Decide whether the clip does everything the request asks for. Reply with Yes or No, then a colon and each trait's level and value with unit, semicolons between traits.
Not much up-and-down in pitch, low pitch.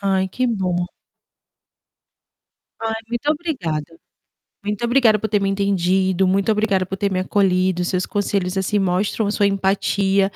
No: narrow, 1.9 semitones; high, 195 Hz